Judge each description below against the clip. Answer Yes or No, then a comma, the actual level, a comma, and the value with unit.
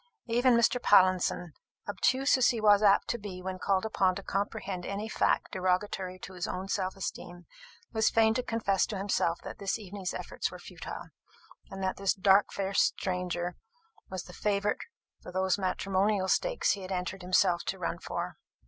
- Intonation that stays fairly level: Yes, narrow, 2.1 semitones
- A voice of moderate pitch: No, high, 195 Hz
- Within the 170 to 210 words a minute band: Yes, average, 175 wpm